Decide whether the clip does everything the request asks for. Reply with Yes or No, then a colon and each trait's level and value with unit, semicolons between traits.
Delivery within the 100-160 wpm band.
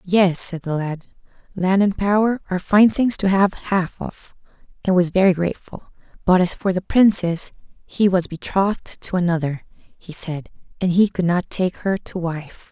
No: average, 180 wpm